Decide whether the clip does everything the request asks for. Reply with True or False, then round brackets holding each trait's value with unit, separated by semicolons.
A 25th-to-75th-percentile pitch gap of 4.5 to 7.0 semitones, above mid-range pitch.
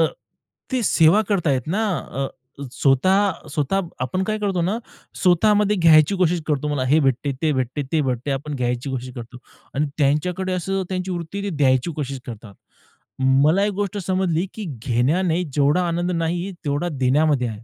False (5.4 semitones; 160 Hz)